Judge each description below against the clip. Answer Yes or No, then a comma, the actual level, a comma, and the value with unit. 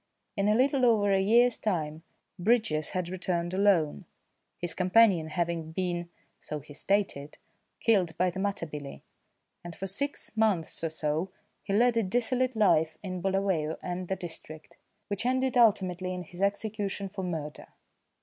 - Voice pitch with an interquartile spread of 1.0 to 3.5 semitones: No, average, 4.0 semitones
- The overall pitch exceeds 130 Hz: Yes, medium, 185 Hz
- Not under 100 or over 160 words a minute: Yes, average, 150 wpm